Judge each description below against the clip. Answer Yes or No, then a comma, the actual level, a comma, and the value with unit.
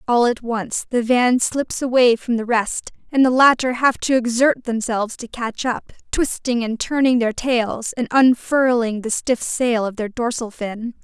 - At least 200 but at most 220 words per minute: No, average, 185 wpm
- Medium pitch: No, high, 240 Hz